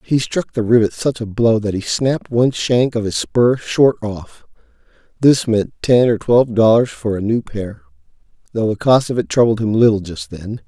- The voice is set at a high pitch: No, low, 110 Hz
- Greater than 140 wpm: Yes, average, 200 wpm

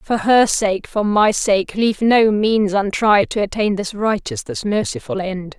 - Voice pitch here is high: Yes, high, 205 Hz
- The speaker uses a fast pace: No, average, 185 wpm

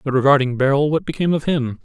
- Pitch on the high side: No, medium, 140 Hz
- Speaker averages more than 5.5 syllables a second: Yes, 7.0 syllables/s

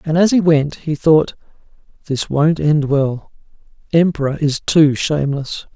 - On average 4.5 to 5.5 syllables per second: No, 4.2 syllables/s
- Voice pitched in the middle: Yes, medium, 150 Hz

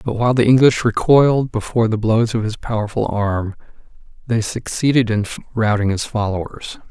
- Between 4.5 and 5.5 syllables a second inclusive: Yes, 5.4 syllables/s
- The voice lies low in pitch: Yes, low, 115 Hz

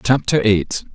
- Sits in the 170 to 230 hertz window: No, low, 115 Hz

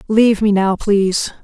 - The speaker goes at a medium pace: Yes, average, 170 wpm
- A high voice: Yes, high, 205 Hz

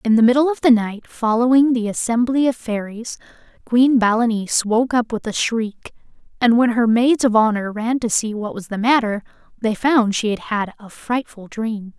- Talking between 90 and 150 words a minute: No, average, 195 wpm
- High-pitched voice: Yes, high, 230 Hz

